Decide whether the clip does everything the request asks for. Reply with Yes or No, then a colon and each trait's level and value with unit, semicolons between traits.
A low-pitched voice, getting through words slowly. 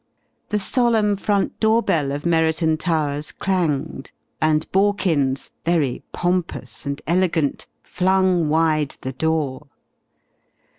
No: medium, 160 Hz; slow, 105 wpm